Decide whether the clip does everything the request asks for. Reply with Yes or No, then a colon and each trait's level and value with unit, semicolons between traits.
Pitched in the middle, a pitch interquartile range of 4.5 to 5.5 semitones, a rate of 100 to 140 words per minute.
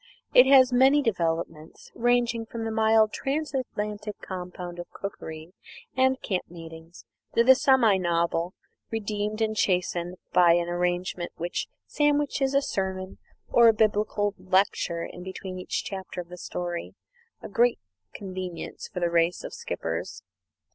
No: high, 195 Hz; average, 4.9 semitones; slow, 135 wpm